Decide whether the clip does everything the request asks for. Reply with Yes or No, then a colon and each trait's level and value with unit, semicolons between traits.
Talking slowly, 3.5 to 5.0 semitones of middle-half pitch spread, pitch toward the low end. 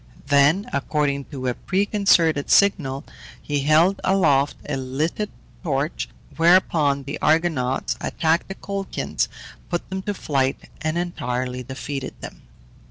No: slow, 120 wpm; average, 4.4 semitones; medium, 150 Hz